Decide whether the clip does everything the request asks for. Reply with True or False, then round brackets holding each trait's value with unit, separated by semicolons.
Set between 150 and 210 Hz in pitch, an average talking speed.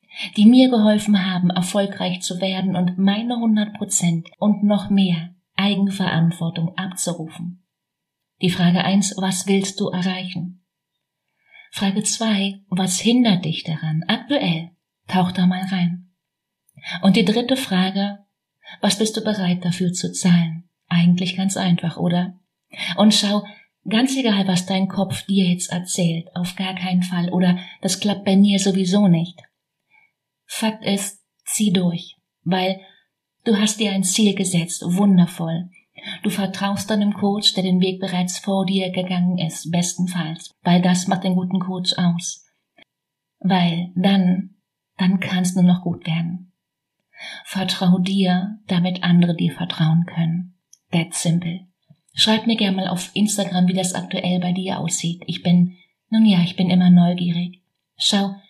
True (185 Hz; 145 wpm)